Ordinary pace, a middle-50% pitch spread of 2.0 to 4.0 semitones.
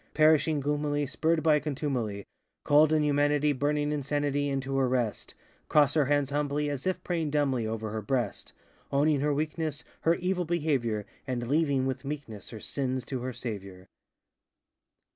Yes: average, 150 wpm; narrow, 2.6 semitones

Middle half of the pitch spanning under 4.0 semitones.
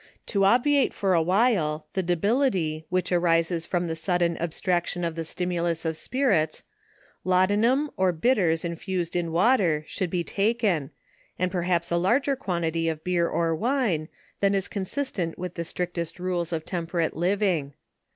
Yes: average, 3.0 semitones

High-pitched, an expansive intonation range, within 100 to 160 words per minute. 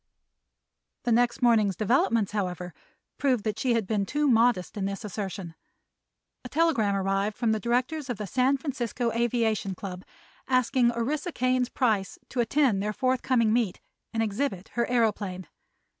No: high, 230 Hz; average, 3.9 semitones; average, 150 wpm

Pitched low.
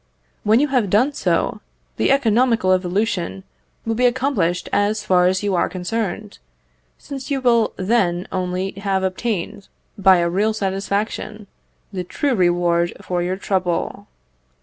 No: high, 195 Hz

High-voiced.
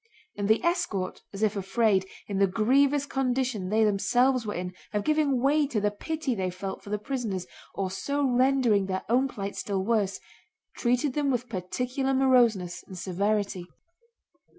Yes: high, 220 Hz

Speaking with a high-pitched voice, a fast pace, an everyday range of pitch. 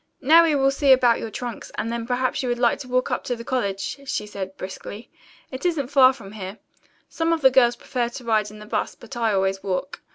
Yes: high, 240 Hz; fast, 240 wpm; average, 3.9 semitones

